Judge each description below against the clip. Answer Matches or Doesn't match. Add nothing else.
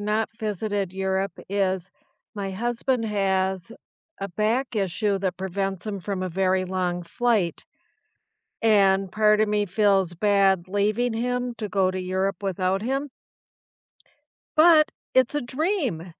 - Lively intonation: Doesn't match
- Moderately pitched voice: Doesn't match